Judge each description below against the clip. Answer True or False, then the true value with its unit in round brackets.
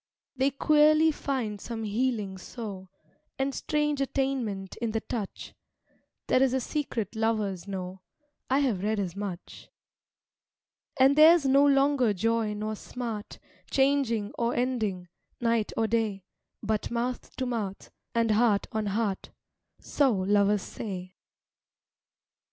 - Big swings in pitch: False (4.4 semitones)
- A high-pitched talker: True (225 Hz)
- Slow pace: True (125 wpm)